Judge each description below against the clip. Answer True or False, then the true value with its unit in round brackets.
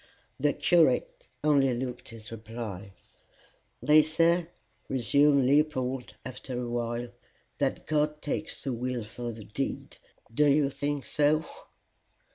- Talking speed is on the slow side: True (120 wpm)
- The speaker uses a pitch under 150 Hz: True (135 Hz)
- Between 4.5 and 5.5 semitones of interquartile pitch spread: False (3.9 semitones)